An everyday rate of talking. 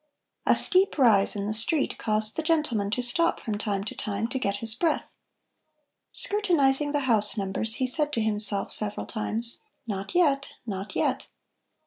Yes: average, 165 wpm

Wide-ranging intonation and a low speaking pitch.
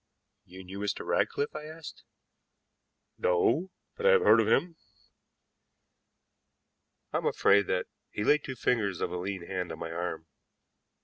Yes: wide, 8.8 semitones; low, 100 Hz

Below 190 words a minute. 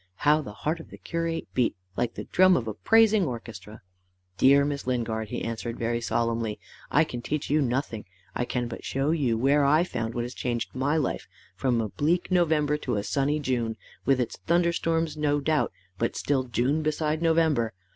No: average, 195 wpm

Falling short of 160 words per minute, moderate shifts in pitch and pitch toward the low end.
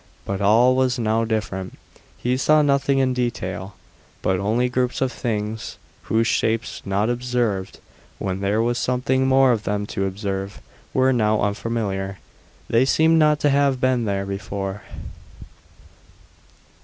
Yes: average, 140 wpm; average, 4.2 semitones; low, 115 Hz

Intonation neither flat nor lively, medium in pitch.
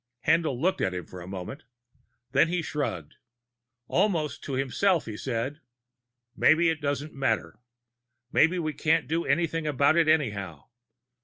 Yes: average, 4.8 semitones; medium, 150 Hz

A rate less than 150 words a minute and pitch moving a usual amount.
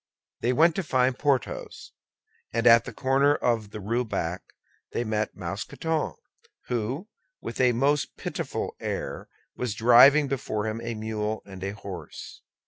Yes: average, 140 wpm; average, 3.8 semitones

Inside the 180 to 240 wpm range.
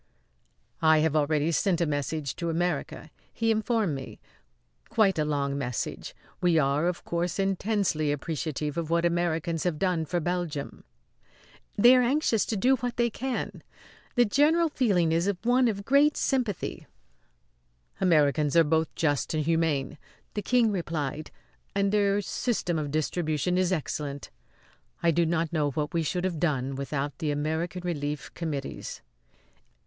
No: average, 150 wpm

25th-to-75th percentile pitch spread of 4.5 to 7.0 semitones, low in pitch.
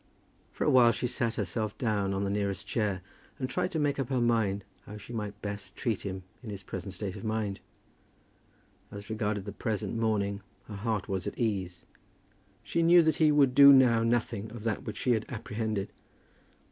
No: average, 2.9 semitones; low, 110 Hz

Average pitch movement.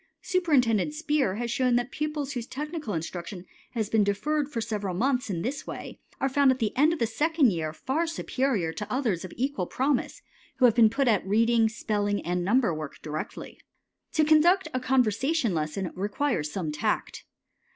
No: wide, 6.0 semitones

